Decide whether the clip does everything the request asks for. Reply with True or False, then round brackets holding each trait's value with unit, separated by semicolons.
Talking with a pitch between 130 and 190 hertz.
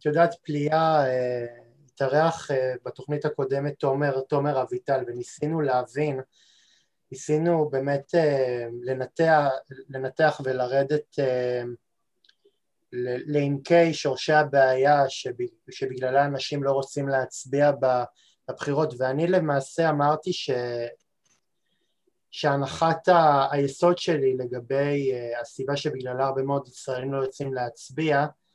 True (140 Hz)